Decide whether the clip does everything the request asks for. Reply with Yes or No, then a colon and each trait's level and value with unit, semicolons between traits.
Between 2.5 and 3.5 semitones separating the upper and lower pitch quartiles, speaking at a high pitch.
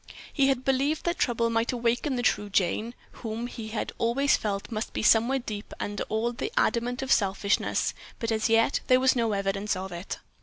Yes: average, 3.1 semitones; high, 230 Hz